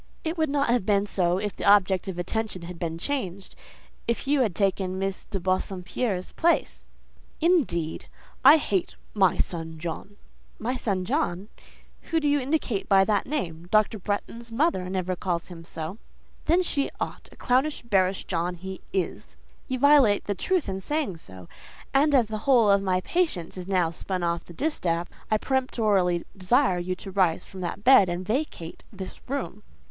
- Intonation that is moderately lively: No, wide, 6.0 semitones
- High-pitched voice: Yes, high, 195 Hz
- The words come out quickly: No, average, 175 wpm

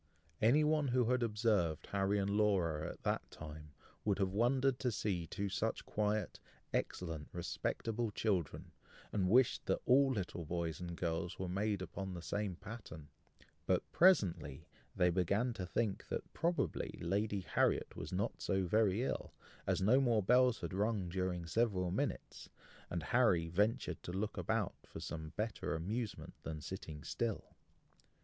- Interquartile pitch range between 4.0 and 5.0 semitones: Yes, average, 4.5 semitones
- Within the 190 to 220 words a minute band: No, average, 155 wpm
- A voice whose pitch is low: Yes, low, 100 Hz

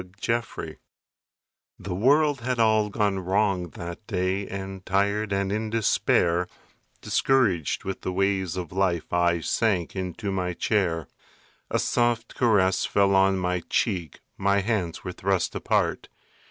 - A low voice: Yes, very low, 95 Hz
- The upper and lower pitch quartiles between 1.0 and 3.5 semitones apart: Yes, average, 2.9 semitones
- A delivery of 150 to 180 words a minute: No, average, 140 wpm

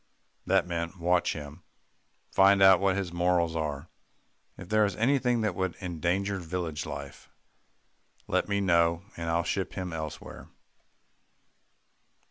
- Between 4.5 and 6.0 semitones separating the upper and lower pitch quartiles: No, narrow, 2.6 semitones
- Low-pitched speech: Yes, very low, 90 Hz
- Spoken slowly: Yes, slow, 125 wpm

